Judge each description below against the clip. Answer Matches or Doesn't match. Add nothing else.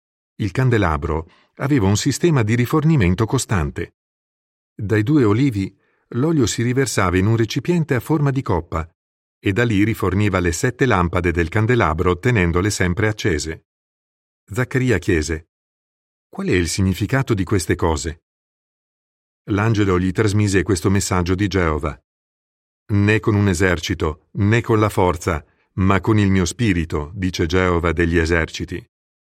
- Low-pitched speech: Matches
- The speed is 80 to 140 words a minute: Matches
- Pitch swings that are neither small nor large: Matches